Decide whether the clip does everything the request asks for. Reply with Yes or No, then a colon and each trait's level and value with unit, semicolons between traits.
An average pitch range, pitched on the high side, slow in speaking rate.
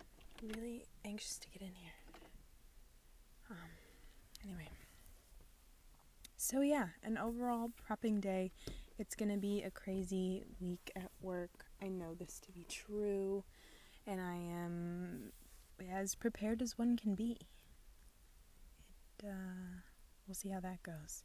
Yes: average, 3.1 semitones; high, 195 Hz; slow, 125 wpm